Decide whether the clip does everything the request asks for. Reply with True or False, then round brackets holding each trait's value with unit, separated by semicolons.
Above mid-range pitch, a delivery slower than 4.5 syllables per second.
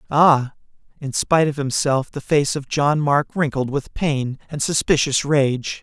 False (140 Hz; 4.2 syllables/s)